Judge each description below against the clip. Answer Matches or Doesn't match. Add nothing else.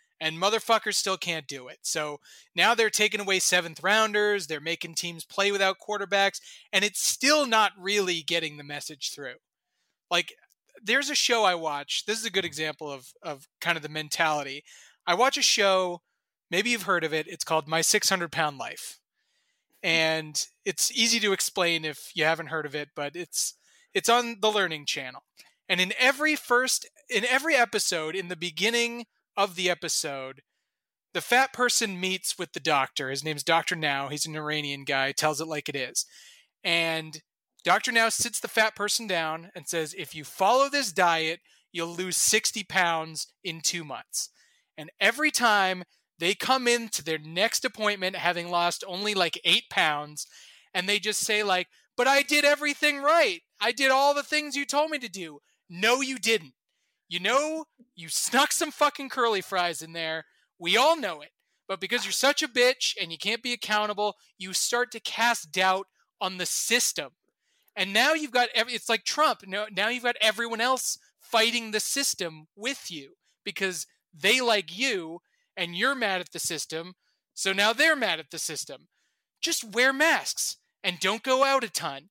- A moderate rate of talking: Matches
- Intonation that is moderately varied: Doesn't match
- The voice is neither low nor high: Doesn't match